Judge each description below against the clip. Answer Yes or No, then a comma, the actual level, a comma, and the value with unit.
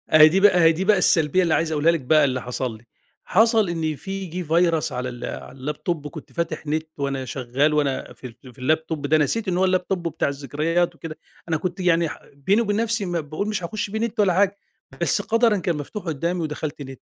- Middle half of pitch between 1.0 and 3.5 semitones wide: No, average, 4.1 semitones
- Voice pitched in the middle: Yes, medium, 165 Hz